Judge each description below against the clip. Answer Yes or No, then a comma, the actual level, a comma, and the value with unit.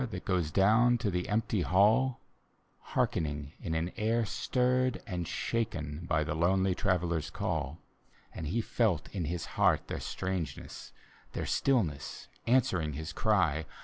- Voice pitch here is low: Yes, very low, 90 Hz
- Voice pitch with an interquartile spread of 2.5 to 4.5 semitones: No, wide, 5.6 semitones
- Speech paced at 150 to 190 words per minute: No, average, 140 wpm